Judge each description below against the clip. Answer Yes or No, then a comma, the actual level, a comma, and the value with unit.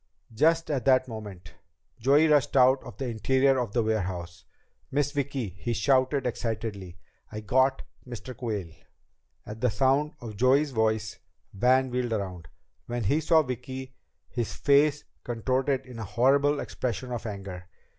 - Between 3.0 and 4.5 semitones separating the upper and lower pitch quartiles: Yes, average, 3.7 semitones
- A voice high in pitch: No, low, 125 Hz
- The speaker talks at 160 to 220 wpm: No, average, 145 wpm